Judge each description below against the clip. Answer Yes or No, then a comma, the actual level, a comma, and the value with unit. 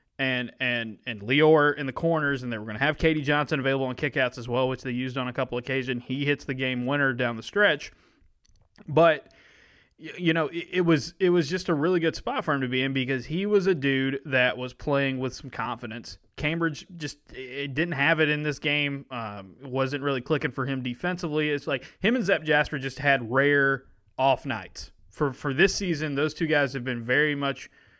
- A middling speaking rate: No, fast, 220 wpm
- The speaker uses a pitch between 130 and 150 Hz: Yes, medium, 140 Hz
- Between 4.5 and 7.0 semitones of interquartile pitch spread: No, average, 3.3 semitones